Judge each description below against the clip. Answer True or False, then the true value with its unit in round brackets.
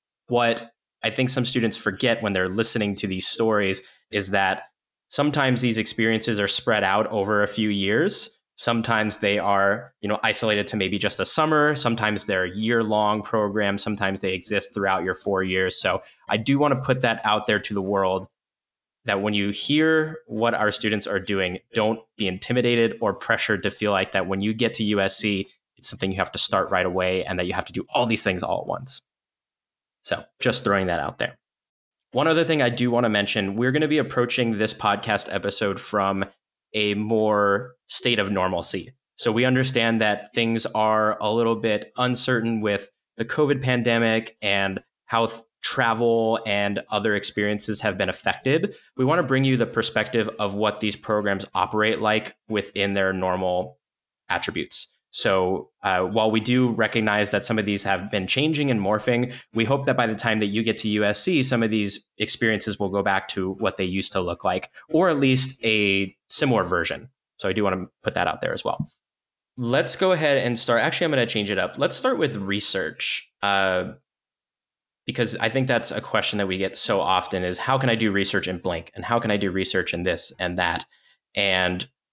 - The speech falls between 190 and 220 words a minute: True (200 wpm)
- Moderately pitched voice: False (105 Hz)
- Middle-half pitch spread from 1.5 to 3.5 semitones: True (3.0 semitones)